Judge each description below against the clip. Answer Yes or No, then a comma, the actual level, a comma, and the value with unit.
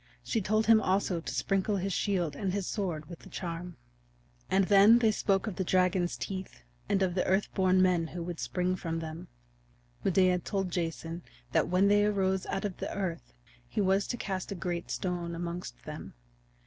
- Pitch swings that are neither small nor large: No, narrow, 2.2 semitones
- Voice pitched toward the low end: No, medium, 185 Hz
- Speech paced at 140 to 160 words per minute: No, average, 190 wpm